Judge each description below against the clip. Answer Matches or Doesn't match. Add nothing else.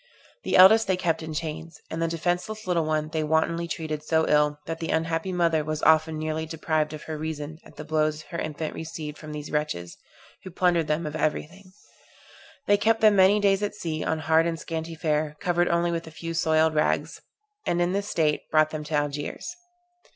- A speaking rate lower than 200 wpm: Doesn't match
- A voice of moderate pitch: Matches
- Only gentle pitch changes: Matches